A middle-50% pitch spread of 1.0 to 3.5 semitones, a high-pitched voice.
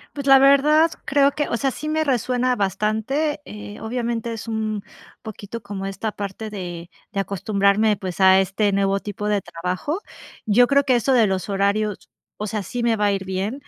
No: average, 4.2 semitones; high, 215 Hz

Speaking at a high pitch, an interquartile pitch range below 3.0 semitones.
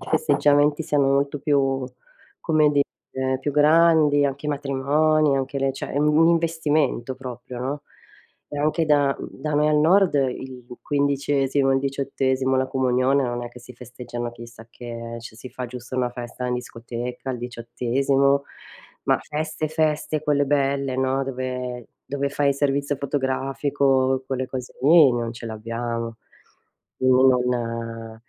No: low, 135 Hz; narrow, 2.6 semitones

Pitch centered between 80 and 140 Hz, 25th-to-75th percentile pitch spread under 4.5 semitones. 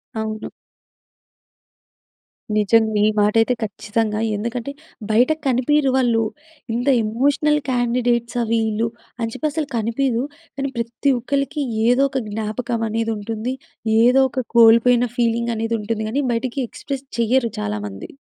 No: high, 235 Hz; narrow, 2.5 semitones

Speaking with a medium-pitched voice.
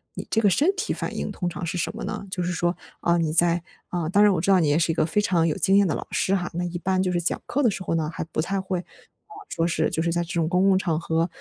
Yes: medium, 175 Hz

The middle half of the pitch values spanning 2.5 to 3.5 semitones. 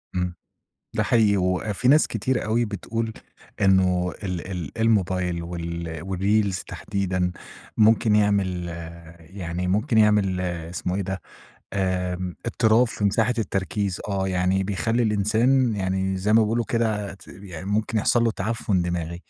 Yes: average, 3.1 semitones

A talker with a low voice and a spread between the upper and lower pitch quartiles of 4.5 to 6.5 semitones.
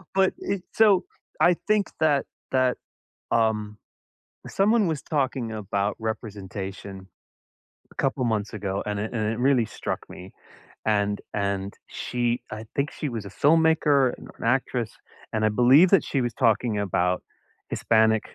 Yes: low, 115 Hz; average, 5.2 semitones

